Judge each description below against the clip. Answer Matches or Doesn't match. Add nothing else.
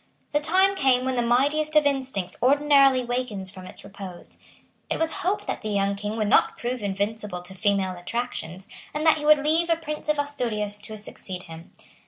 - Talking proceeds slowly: Doesn't match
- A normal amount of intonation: Doesn't match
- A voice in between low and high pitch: Doesn't match